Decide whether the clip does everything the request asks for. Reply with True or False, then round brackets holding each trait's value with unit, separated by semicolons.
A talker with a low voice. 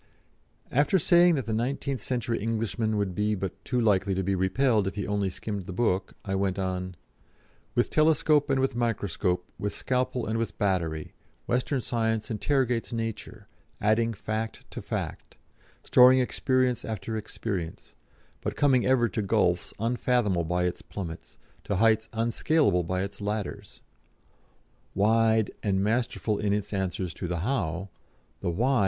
True (110 Hz)